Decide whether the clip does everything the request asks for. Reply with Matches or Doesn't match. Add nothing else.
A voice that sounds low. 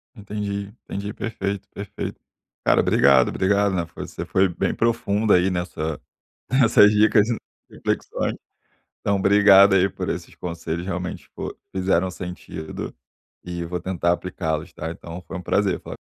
Matches